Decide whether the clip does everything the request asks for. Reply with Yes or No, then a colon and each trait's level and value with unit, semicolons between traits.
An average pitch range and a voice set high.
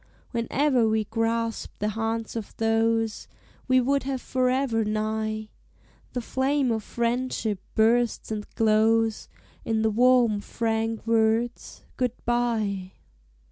No: narrow, 1.8 semitones; high, 225 Hz